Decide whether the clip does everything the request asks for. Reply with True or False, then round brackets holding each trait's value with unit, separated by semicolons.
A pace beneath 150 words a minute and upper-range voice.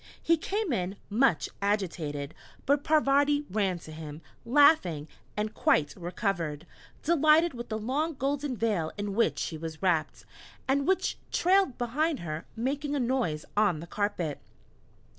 True (140 wpm; 215 Hz)